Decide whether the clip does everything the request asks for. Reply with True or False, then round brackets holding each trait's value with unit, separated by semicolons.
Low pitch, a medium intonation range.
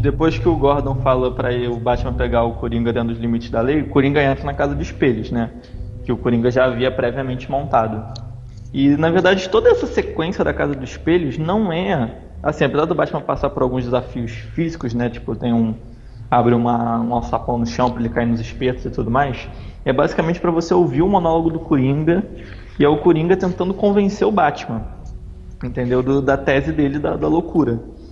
True (125 Hz; 4.0 semitones)